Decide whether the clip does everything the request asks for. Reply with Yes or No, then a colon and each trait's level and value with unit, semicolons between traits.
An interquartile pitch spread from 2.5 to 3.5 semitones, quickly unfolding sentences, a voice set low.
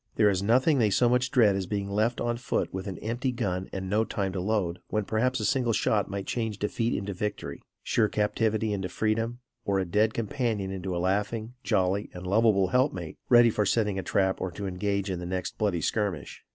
Yes: average, 3.1 semitones; fast, 220 wpm; low, 105 Hz